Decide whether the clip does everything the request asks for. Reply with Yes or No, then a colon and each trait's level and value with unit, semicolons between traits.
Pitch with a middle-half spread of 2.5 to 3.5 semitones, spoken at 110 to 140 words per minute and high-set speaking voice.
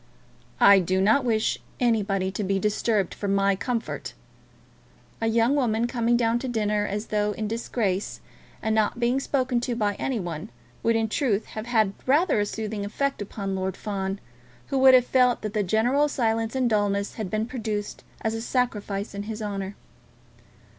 No: average, 2.9 semitones; average, 175 wpm; high, 220 Hz